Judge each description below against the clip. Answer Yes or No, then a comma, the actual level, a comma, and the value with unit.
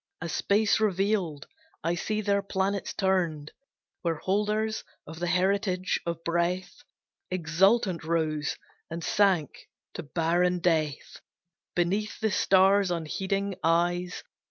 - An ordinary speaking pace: No, slow, 110 wpm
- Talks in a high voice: No, medium, 180 Hz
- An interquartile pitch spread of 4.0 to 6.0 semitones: No, average, 3.0 semitones